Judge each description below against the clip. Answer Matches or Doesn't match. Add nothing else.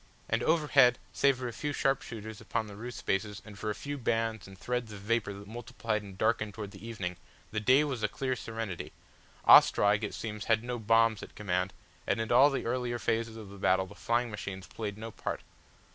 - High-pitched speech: Doesn't match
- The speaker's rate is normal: Doesn't match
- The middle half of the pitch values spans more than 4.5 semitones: Doesn't match